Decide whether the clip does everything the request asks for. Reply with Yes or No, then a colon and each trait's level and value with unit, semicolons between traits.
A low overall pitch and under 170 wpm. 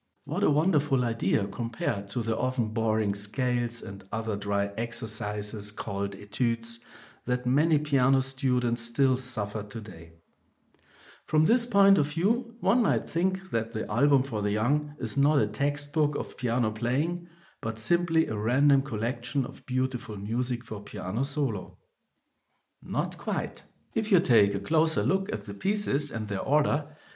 Yes: low, 125 Hz; average, 150 wpm